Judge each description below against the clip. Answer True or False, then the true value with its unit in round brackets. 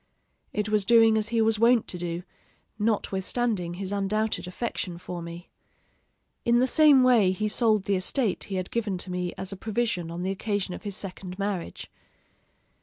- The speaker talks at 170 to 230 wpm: True (180 wpm)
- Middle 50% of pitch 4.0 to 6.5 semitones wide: False (3.5 semitones)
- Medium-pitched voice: False (200 Hz)